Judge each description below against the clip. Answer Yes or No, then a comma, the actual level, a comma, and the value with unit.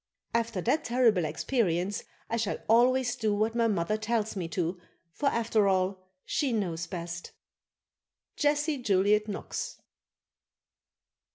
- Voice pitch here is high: Yes, high, 210 Hz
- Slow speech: Yes, slow, 120 wpm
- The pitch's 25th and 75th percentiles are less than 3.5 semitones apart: No, average, 4.0 semitones